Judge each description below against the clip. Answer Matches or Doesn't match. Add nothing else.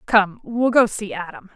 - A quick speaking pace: Doesn't match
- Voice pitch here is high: Matches